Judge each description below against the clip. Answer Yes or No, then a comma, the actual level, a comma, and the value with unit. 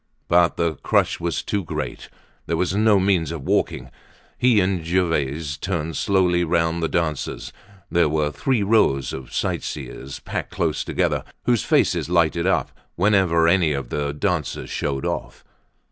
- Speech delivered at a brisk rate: No, average, 150 wpm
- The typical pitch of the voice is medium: No, very low, 85 Hz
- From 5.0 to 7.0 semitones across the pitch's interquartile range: No, average, 3.7 semitones